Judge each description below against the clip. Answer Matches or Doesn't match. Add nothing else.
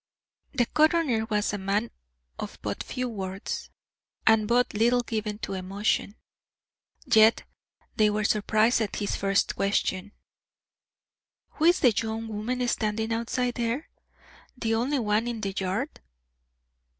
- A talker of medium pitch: Doesn't match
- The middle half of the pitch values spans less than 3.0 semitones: Matches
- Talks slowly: Matches